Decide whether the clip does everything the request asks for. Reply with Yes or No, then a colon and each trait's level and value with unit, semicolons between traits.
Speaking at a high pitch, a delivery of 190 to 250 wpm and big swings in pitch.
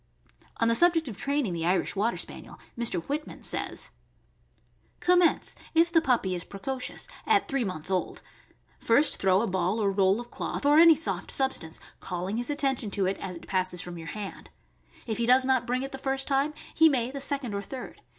Yes: high, 240 Hz; average, 200 wpm; wide, 6.5 semitones